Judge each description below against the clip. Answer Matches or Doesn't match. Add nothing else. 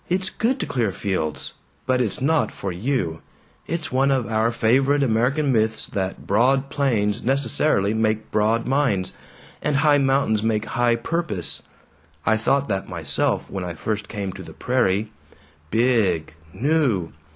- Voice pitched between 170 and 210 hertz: Doesn't match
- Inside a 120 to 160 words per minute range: Matches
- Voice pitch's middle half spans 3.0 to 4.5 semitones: Doesn't match